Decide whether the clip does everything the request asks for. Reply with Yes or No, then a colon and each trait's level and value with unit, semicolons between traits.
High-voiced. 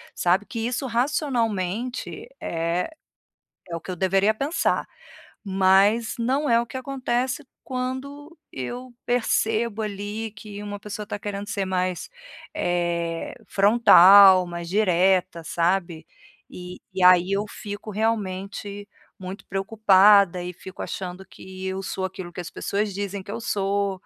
Yes: high, 200 Hz